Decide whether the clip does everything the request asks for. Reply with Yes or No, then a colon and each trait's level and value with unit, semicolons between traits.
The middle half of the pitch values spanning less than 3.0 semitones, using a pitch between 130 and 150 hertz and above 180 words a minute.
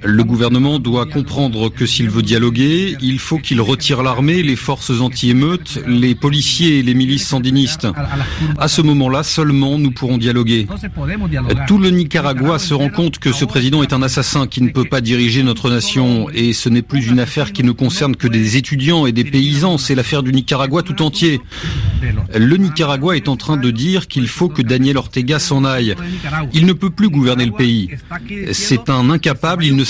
No: average, 3.5 semitones; low, 135 Hz; average, 190 wpm